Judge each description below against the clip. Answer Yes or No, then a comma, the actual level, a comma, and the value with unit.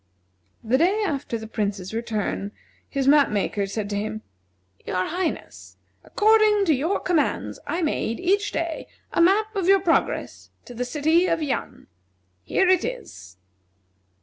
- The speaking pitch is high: Yes, very high, 305 Hz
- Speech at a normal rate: Yes, average, 150 wpm